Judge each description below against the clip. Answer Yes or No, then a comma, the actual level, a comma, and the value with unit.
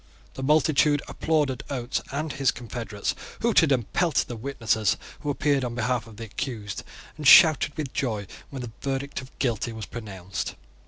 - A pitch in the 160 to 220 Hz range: No, low, 130 Hz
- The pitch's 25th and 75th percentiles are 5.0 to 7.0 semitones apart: No, average, 4.0 semitones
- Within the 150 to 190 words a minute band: Yes, average, 165 wpm